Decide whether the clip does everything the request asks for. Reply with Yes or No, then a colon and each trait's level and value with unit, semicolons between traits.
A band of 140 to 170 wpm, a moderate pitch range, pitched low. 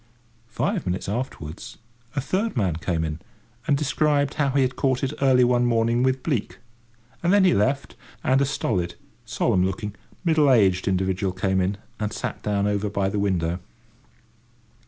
No: average, 165 wpm; wide, 6.1 semitones; low, 115 Hz